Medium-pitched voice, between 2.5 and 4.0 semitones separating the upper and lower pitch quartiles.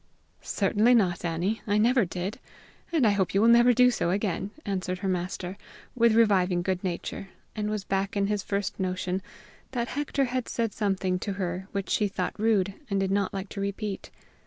No: high, 200 Hz; average, 2.8 semitones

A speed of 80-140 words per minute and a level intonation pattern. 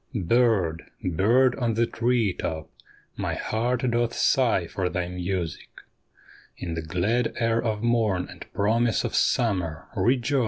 No: slow, 135 wpm; average, 4.9 semitones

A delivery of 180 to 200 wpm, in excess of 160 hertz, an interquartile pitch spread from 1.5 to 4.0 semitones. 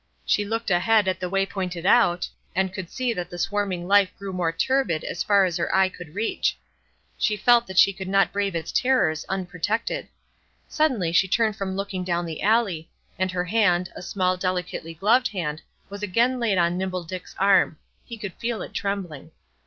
Yes: average, 190 wpm; high, 190 Hz; average, 2.8 semitones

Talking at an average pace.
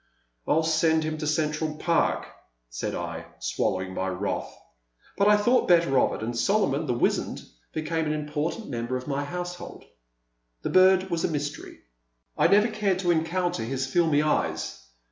Yes: average, 175 wpm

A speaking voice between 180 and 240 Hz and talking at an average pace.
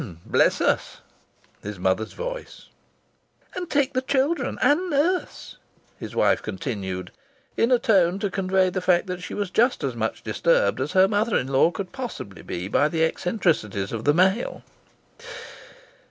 Yes: high, 190 Hz; average, 155 wpm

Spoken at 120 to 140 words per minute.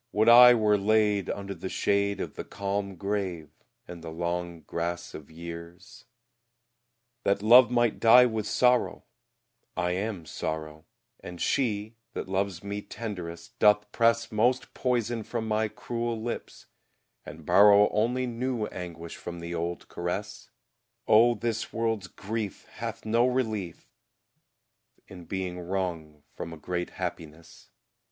Yes: slow, 135 wpm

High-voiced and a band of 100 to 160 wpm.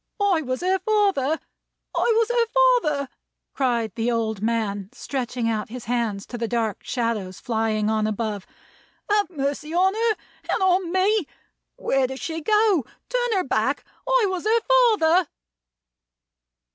Yes: very high, 285 Hz; average, 145 wpm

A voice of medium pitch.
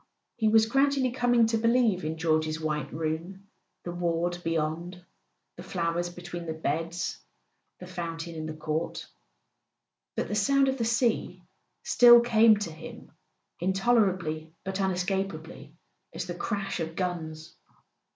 Yes: medium, 175 Hz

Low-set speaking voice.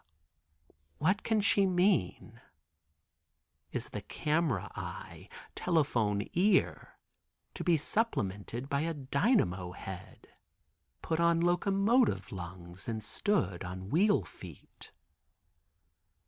No: medium, 150 Hz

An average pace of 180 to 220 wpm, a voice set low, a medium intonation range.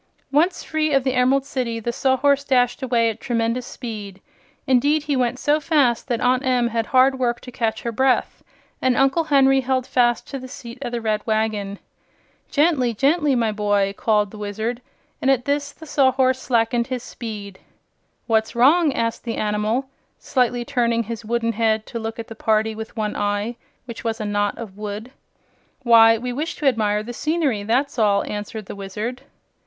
No: average, 185 wpm; high, 240 Hz; average, 3.1 semitones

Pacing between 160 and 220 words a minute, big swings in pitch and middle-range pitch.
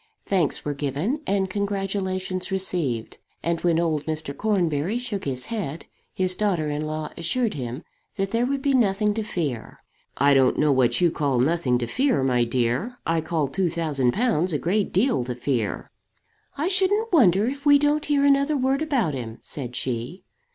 Yes: average, 180 wpm; wide, 7.9 semitones; medium, 175 Hz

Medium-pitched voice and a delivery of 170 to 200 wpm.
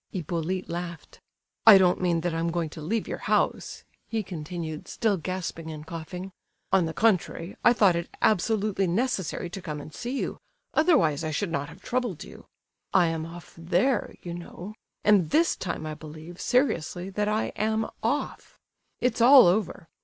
Yes: medium, 180 Hz; average, 175 wpm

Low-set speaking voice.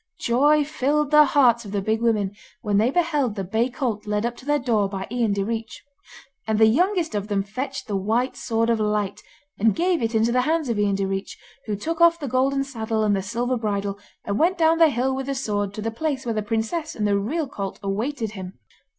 No: high, 230 Hz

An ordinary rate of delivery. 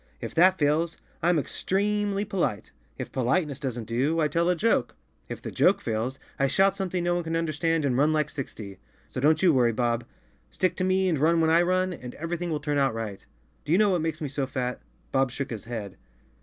No: fast, 225 wpm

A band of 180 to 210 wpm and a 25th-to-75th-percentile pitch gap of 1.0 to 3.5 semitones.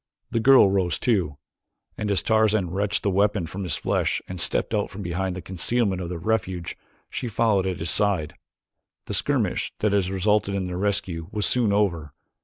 Yes: average, 190 wpm; average, 2.7 semitones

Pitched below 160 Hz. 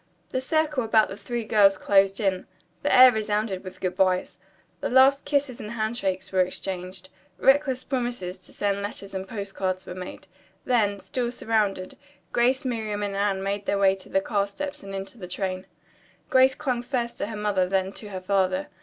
No: high, 205 Hz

